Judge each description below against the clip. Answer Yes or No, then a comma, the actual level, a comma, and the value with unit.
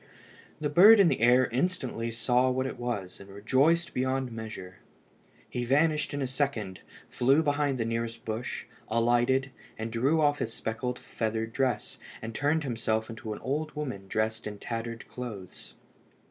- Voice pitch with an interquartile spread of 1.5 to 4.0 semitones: Yes, average, 3.7 semitones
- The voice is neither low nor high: No, low, 120 Hz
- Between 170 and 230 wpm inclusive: No, average, 160 wpm